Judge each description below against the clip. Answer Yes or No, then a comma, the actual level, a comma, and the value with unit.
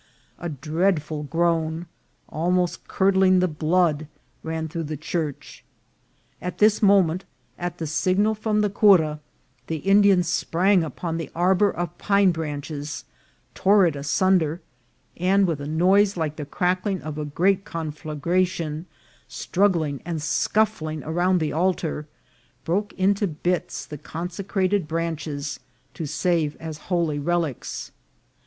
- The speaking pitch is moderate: Yes, medium, 170 Hz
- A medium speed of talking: No, slow, 130 wpm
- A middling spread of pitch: Yes, average, 3.3 semitones